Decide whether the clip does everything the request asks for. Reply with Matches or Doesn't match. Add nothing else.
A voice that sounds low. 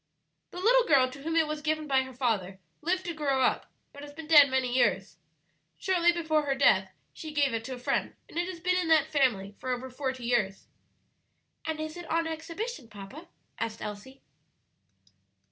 Doesn't match